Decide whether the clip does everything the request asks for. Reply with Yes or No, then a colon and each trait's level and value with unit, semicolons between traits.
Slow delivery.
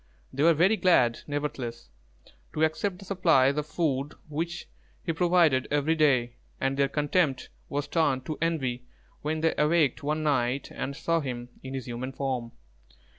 No: average, 160 wpm